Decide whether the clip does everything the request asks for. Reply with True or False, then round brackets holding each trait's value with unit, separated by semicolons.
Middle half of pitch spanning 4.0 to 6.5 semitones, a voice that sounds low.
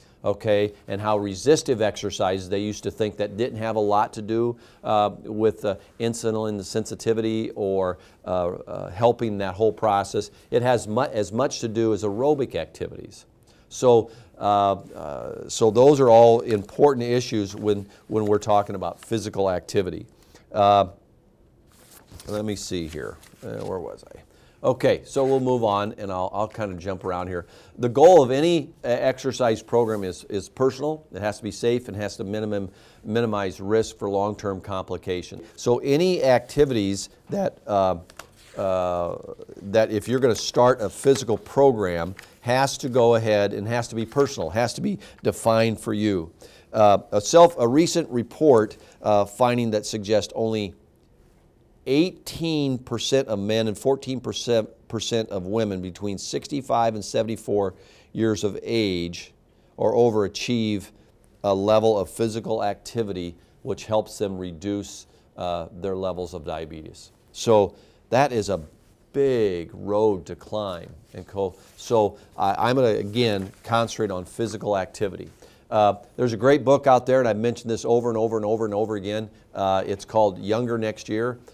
False (3.0 semitones; 110 Hz)